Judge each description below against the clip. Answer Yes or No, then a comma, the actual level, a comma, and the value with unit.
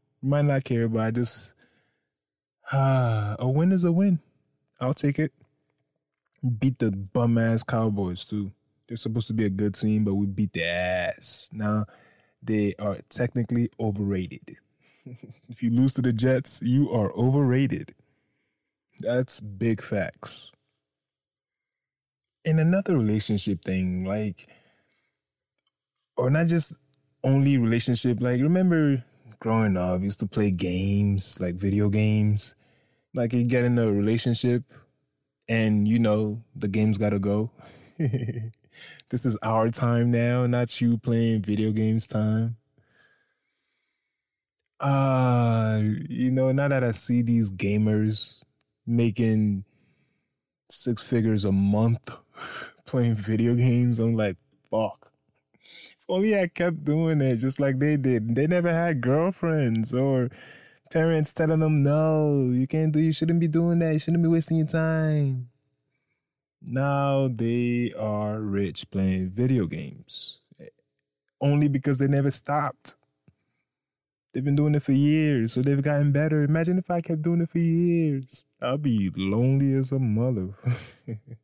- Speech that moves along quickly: No, average, 140 wpm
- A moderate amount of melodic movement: Yes, average, 4.4 semitones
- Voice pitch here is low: Yes, low, 125 Hz